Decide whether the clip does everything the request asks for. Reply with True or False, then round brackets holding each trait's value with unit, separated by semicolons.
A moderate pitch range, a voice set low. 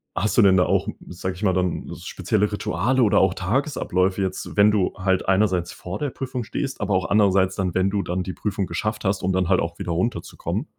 False (2.3 semitones; 95 Hz)